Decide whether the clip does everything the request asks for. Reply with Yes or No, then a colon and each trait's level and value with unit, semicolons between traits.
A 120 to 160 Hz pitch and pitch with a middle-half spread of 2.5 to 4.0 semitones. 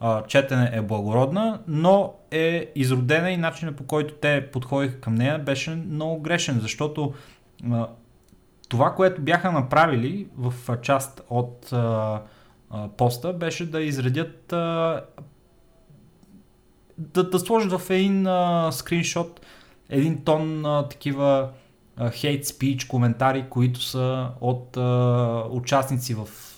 No: medium, 140 Hz; average, 4.9 semitones